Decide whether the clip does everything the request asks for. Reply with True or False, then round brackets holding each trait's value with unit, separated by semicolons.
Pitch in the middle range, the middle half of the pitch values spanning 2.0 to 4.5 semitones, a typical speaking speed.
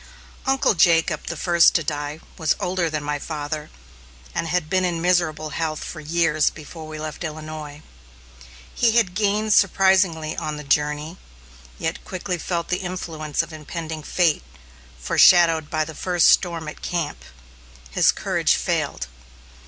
True (160 Hz; 2.5 semitones; 150 wpm)